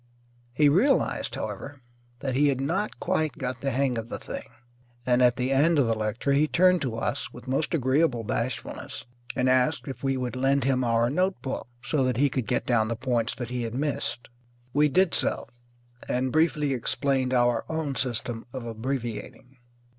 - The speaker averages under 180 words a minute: No, average, 185 wpm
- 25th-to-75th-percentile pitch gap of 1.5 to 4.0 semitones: Yes, average, 2.8 semitones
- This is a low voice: Yes, low, 130 Hz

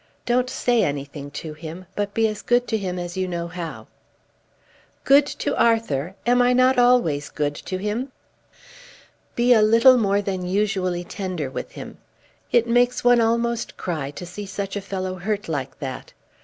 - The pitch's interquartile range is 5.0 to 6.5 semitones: Yes, wide, 5.4 semitones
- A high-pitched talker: Yes, high, 200 Hz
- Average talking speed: Yes, average, 170 wpm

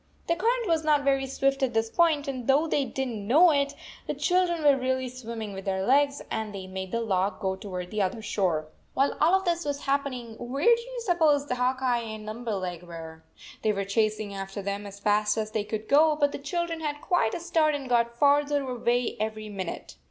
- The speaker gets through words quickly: Yes, fast, 225 wpm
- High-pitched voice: Yes, very high, 250 Hz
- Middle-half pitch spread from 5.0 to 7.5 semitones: Yes, wide, 5.6 semitones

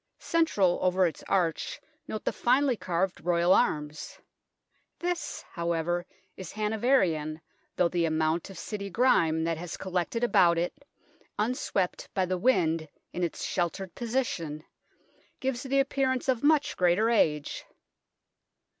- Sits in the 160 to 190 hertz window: Yes, medium, 185 Hz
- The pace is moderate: No, slow, 130 wpm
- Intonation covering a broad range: Yes, wide, 6.2 semitones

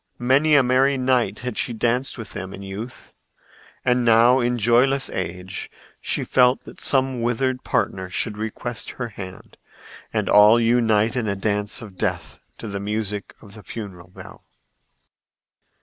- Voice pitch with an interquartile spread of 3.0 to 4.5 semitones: Yes, average, 3.5 semitones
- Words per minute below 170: Yes, average, 155 wpm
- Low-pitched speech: Yes, low, 115 Hz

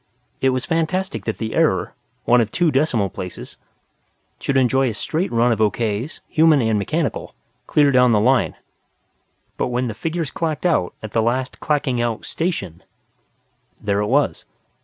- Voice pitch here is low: Yes, low, 125 Hz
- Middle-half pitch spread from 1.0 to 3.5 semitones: No, wide, 5.6 semitones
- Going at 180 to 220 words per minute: No, average, 160 wpm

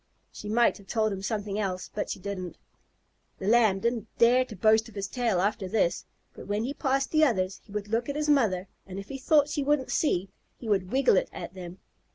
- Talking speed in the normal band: No, fast, 225 wpm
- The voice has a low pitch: No, high, 215 Hz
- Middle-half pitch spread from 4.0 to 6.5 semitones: Yes, average, 4.4 semitones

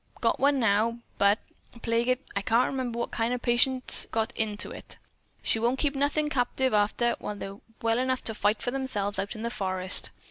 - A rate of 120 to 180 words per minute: No, average, 200 wpm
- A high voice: Yes, high, 235 Hz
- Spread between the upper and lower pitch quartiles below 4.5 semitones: Yes, average, 3.6 semitones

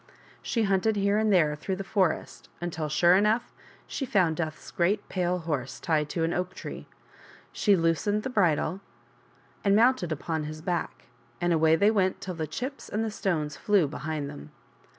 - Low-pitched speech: No, medium, 180 Hz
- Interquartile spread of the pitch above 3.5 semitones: Yes, average, 4.4 semitones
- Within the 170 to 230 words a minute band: Yes, average, 175 wpm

